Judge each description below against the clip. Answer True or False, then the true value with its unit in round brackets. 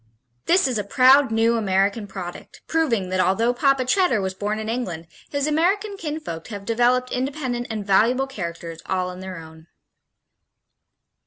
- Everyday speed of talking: True (155 wpm)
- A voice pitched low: False (230 Hz)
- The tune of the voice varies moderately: False (6.0 semitones)